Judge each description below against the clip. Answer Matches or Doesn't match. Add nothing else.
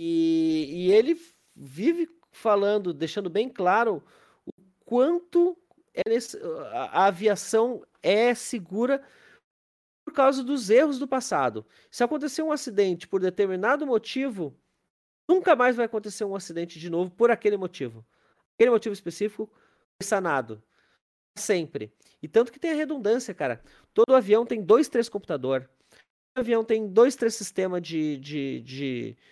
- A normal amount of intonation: Doesn't match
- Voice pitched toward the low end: Doesn't match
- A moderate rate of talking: Matches